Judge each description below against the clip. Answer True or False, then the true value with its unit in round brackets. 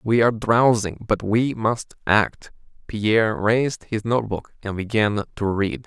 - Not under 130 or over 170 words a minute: True (155 wpm)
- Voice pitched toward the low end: True (110 Hz)